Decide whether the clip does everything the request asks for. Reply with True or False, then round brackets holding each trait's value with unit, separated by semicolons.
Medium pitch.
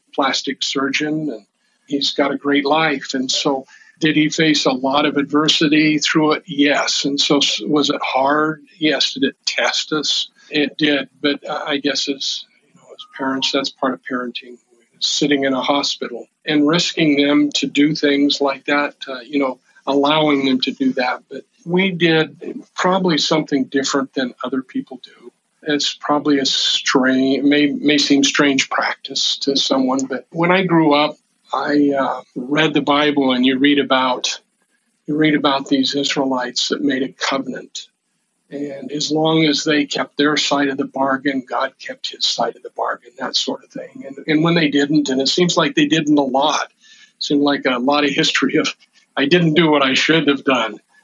True (145 Hz)